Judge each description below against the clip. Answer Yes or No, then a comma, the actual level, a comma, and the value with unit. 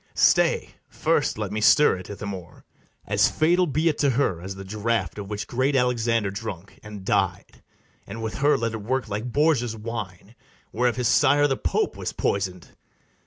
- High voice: No, low, 115 Hz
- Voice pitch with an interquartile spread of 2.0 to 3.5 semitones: No, average, 4.5 semitones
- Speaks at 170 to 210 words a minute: Yes, average, 180 wpm